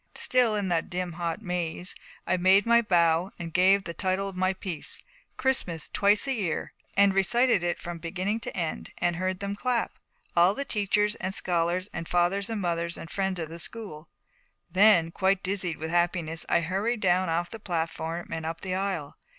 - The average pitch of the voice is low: No, medium, 185 Hz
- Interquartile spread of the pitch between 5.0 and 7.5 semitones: No, average, 2.9 semitones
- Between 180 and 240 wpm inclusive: Yes, average, 190 wpm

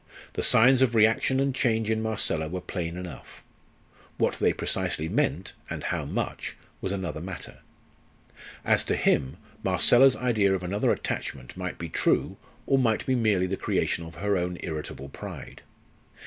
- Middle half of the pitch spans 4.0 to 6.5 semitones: Yes, average, 4.6 semitones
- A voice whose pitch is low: Yes, very low, 95 Hz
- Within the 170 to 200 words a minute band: No, average, 160 wpm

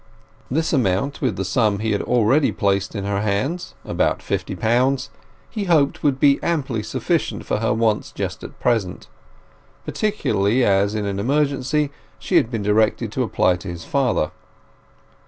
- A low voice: Yes, low, 115 Hz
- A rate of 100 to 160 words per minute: Yes, average, 155 wpm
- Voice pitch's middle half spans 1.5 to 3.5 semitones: No, wide, 5.5 semitones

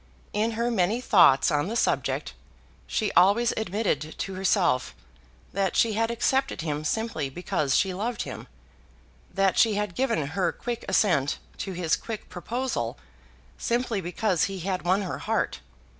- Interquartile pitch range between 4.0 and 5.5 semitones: Yes, average, 4.6 semitones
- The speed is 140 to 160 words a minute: Yes, average, 150 wpm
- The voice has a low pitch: No, high, 195 Hz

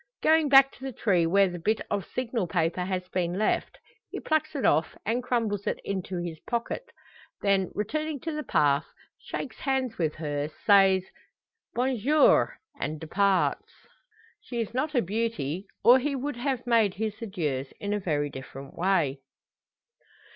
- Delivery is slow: No, average, 160 wpm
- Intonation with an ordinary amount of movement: No, wide, 6.2 semitones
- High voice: Yes, high, 205 Hz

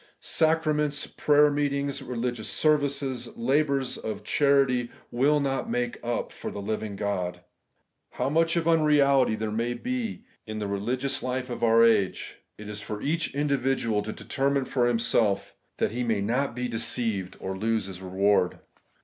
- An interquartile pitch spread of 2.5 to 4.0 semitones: No, average, 4.7 semitones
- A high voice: No, low, 125 Hz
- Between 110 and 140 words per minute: No, average, 160 wpm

